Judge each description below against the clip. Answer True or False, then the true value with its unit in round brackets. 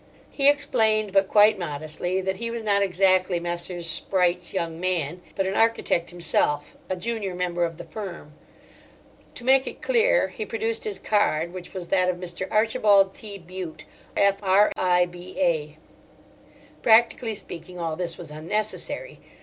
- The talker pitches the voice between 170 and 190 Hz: True (185 Hz)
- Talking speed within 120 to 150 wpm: True (140 wpm)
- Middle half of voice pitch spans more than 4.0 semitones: False (3.7 semitones)